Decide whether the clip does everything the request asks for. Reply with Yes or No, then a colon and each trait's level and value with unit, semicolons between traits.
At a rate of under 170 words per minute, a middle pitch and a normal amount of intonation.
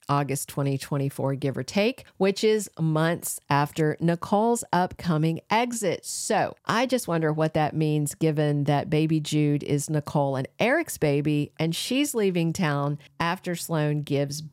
Yes: average, 145 wpm; medium, 155 Hz; average, 3.5 semitones